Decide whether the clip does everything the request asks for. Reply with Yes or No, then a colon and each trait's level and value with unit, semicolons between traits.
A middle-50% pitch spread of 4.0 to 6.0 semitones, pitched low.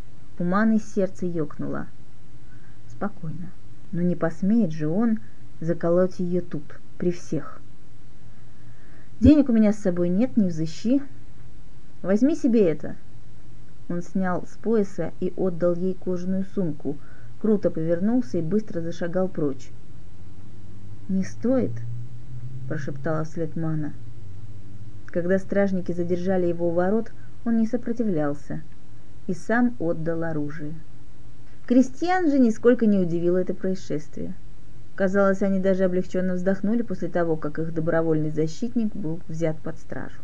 No: average, 4.8 semitones; medium, 175 Hz